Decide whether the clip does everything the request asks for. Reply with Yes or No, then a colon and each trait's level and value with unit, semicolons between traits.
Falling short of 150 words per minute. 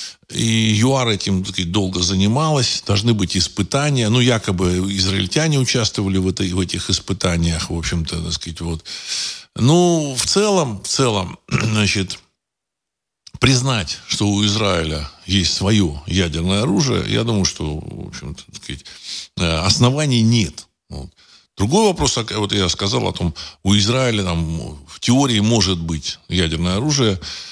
Yes: average, 135 wpm